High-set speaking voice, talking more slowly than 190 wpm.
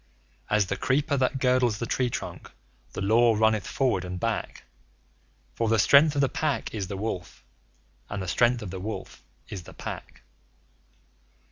No: low, 115 Hz; average, 165 wpm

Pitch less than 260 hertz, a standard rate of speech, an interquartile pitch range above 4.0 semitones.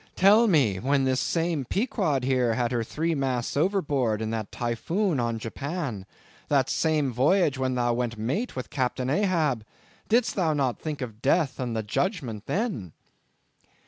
Yes: low, 135 Hz; average, 160 wpm; wide, 5.6 semitones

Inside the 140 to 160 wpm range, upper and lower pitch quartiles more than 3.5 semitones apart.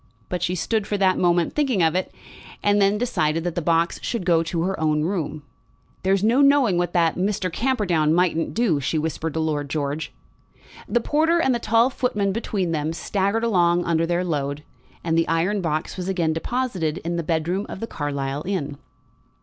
No: average, 190 wpm; average, 4.2 semitones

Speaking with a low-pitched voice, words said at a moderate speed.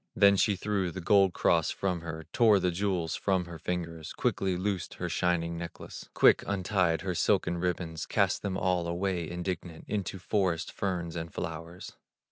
Yes: very low, 90 Hz; average, 165 wpm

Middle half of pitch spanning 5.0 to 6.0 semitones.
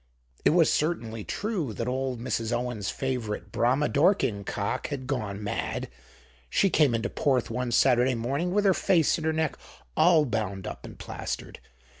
Yes: wide, 5.5 semitones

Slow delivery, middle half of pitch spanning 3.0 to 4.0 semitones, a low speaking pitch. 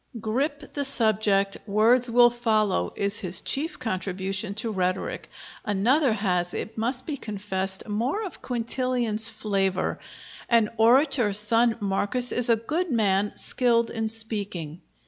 No: slow, 130 wpm; average, 3.6 semitones; high, 220 Hz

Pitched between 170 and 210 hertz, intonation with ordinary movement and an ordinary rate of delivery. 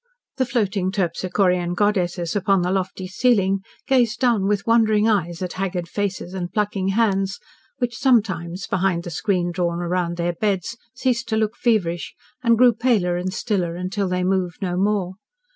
Yes: high, 190 Hz; average, 3.3 semitones; average, 160 wpm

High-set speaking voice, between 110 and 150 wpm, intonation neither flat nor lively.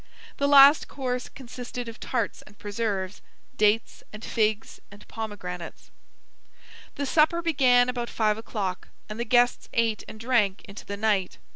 Yes: high, 225 Hz; average, 145 wpm; average, 3.2 semitones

